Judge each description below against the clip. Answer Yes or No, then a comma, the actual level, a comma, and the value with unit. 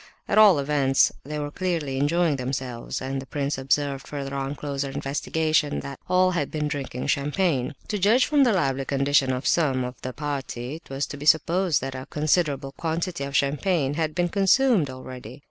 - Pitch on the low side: No, medium, 145 Hz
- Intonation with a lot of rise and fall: No, average, 3.5 semitones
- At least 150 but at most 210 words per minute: Yes, average, 180 wpm